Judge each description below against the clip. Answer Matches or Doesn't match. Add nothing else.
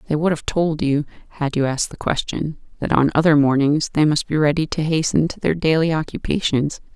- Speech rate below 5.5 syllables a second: Doesn't match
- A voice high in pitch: Doesn't match